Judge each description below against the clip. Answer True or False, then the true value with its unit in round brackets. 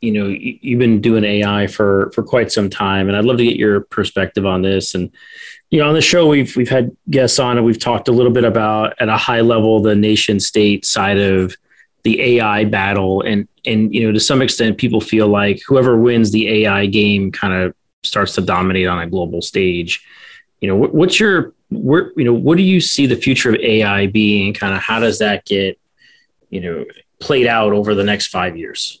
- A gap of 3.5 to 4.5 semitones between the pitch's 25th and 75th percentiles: False (3.1 semitones)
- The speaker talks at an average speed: False (220 wpm)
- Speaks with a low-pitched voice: True (110 Hz)